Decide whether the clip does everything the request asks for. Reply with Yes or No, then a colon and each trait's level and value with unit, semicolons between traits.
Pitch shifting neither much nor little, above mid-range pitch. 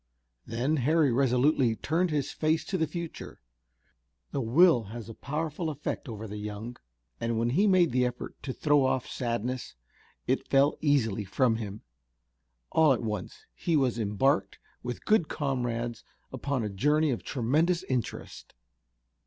No: average, 4.8 semitones; low, 130 Hz